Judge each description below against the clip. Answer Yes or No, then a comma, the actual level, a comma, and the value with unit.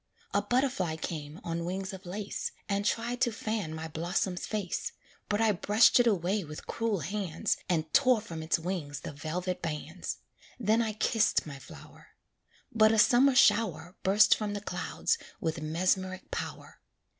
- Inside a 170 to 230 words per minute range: No, average, 160 wpm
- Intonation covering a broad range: No, average, 4.7 semitones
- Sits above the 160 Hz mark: Yes, high, 190 Hz